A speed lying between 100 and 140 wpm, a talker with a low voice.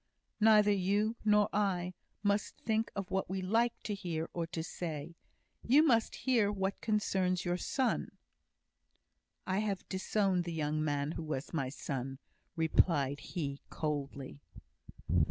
No: slow, 135 wpm; medium, 185 Hz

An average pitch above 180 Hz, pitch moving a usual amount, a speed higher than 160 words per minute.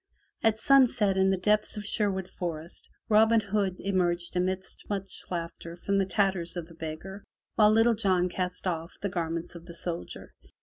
Yes: high, 190 Hz; average, 3.1 semitones; average, 170 wpm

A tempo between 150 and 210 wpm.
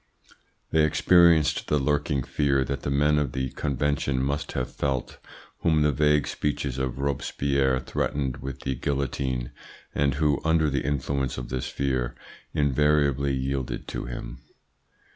No: average, 140 wpm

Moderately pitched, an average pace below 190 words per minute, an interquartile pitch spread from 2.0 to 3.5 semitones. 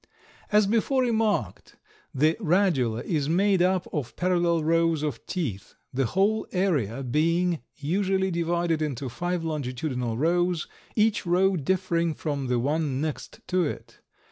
No: medium, 165 Hz; slow, 135 wpm; average, 4.3 semitones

